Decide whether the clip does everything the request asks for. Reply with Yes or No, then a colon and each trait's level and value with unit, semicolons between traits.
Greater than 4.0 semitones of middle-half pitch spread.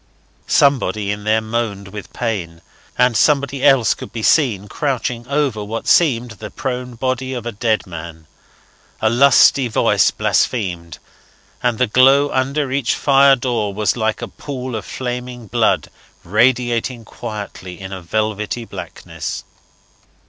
No: average, 3.7 semitones